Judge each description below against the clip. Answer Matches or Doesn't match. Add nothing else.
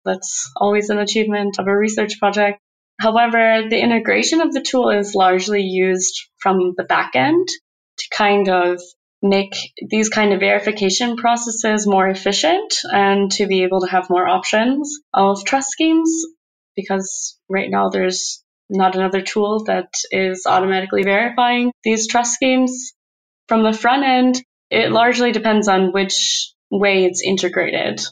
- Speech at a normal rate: Matches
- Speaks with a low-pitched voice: Doesn't match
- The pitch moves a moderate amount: Matches